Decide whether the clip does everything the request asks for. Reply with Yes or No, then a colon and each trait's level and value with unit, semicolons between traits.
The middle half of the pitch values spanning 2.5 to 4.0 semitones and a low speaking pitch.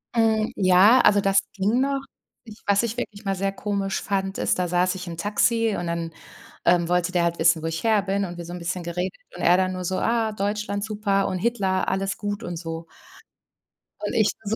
No: average, 2.8 semitones; high, 195 Hz